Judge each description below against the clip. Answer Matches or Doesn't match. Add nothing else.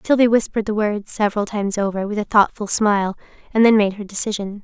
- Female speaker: Matches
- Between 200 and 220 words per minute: Matches